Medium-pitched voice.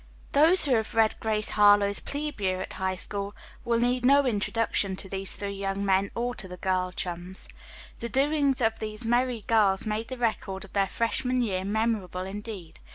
No: high, 210 Hz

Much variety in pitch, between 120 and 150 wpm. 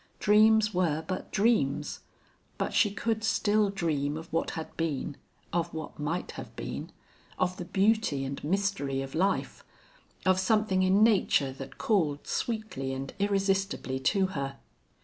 Yes: wide, 5.9 semitones; average, 145 wpm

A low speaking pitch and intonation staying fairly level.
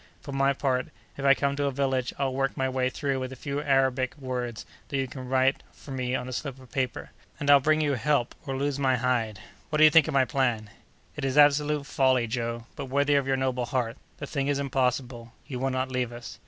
Yes: low, 130 Hz; narrow, 1.7 semitones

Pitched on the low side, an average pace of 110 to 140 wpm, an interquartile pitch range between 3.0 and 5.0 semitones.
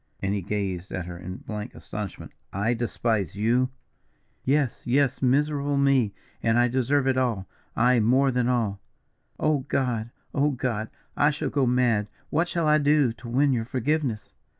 No: low, 125 Hz; average, 165 wpm; average, 4.3 semitones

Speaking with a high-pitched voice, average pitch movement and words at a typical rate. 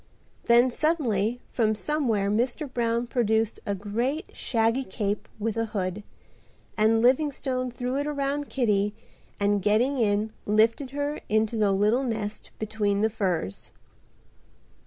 No: high, 225 Hz; average, 3.6 semitones; slow, 130 wpm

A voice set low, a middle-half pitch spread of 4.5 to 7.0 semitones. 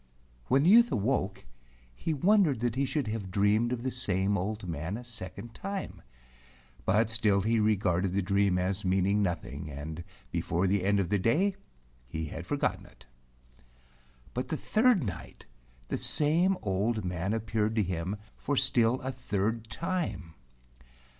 Yes: low, 105 Hz; average, 5.2 semitones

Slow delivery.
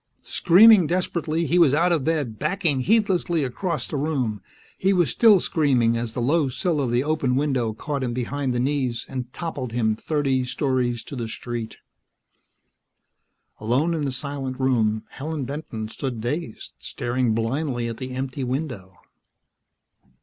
No: average, 155 wpm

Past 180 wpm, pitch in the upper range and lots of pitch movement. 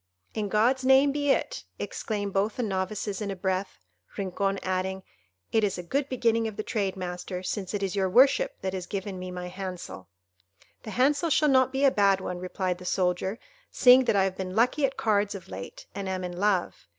No: fast, 205 wpm; high, 195 Hz; average, 3.8 semitones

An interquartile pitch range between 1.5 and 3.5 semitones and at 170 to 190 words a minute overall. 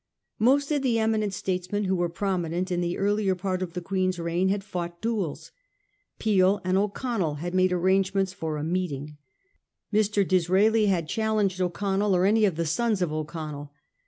Yes: average, 2.9 semitones; average, 175 wpm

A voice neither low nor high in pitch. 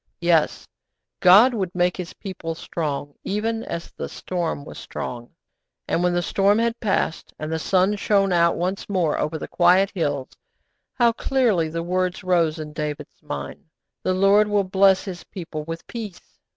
Yes: medium, 180 Hz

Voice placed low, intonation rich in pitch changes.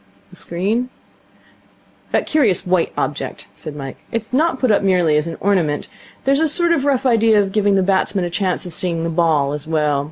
No: high, 190 Hz; wide, 5.7 semitones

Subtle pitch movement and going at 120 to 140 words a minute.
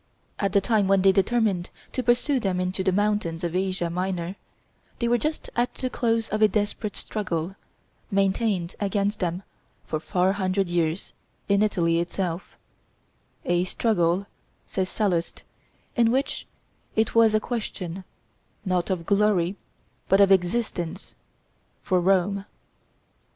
No: average, 3.0 semitones; slow, 135 wpm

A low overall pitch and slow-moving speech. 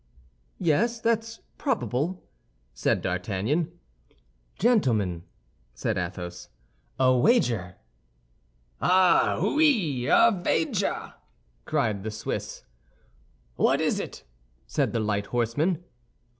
Yes: low, 130 Hz; slow, 90 wpm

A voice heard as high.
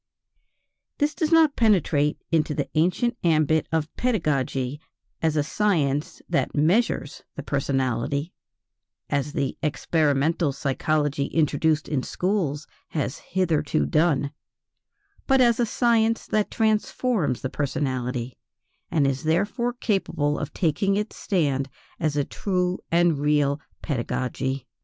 No: medium, 155 Hz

